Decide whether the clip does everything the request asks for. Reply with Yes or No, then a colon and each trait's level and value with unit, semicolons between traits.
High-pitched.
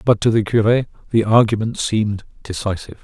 No: low, 110 Hz